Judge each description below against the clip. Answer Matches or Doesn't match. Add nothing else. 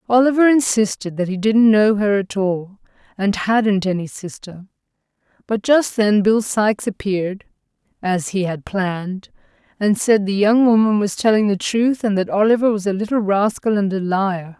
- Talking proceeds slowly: Doesn't match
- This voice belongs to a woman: Matches